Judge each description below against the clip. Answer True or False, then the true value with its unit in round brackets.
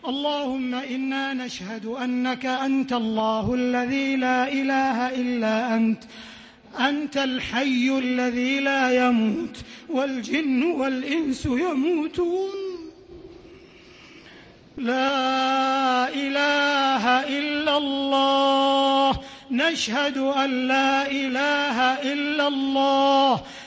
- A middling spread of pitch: False (1.7 semitones)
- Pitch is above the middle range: True (270 Hz)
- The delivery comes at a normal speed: False (75 wpm)